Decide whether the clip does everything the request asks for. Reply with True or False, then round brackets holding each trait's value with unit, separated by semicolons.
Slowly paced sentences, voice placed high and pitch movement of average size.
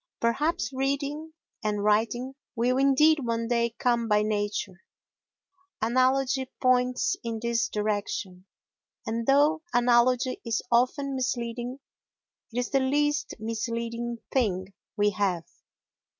True (110 wpm; 240 Hz; 3.1 semitones)